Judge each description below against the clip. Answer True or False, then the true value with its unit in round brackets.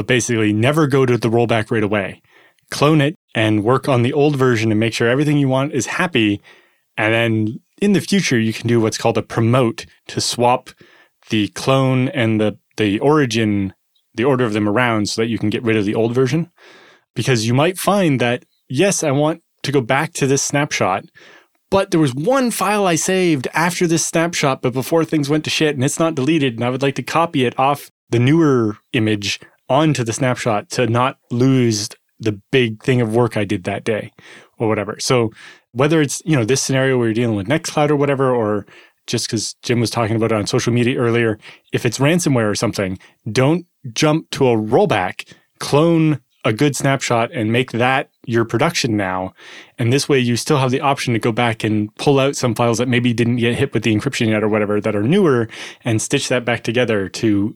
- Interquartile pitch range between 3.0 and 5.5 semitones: True (4.3 semitones)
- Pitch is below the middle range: True (125 Hz)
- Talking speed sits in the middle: False (210 wpm)